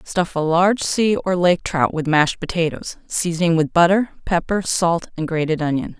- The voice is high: No, medium, 170 Hz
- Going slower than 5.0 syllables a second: Yes, 4.8 syllables/s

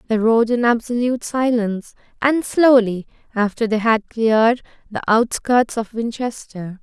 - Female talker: Yes, female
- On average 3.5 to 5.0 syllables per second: Yes, 4.5 syllables/s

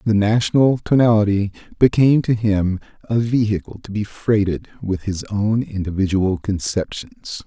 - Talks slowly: Yes, slow, 130 wpm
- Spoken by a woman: No, male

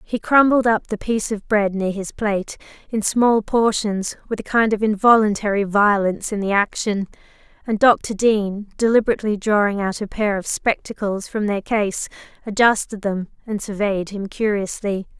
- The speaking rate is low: No, average, 160 wpm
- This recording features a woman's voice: Yes, female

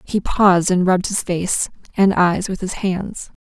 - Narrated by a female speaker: Yes, female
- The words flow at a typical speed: Yes, average, 190 wpm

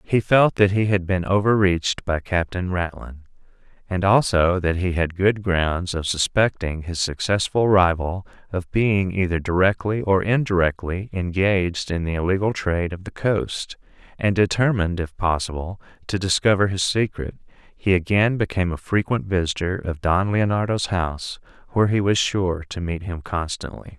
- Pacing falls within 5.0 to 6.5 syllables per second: No, 4.8 syllables/s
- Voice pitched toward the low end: Yes, very low, 95 Hz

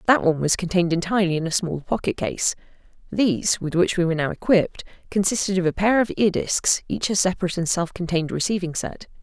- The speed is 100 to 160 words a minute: No, average, 200 wpm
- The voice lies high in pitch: No, medium, 180 Hz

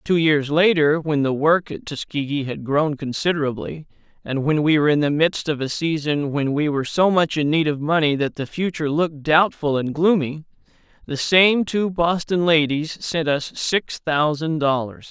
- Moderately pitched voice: Yes, medium, 155 Hz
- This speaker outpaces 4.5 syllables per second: Yes, 4.8 syllables/s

